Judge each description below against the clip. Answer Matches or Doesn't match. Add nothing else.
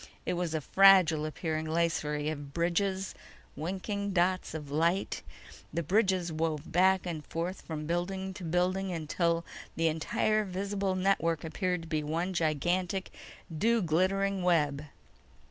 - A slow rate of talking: Matches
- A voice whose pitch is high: Doesn't match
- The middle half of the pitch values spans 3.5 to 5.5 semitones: Doesn't match